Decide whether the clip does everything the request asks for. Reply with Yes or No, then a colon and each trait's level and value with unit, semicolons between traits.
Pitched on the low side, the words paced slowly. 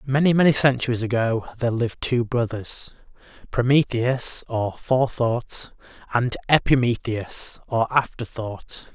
Yes: low, 120 Hz; slow, 100 wpm